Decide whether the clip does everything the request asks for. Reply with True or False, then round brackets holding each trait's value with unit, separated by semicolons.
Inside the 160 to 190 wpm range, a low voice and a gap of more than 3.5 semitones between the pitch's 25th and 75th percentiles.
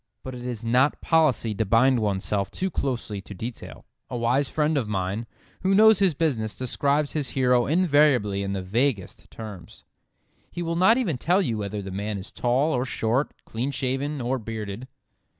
True (180 wpm; 125 Hz; 5.5 semitones)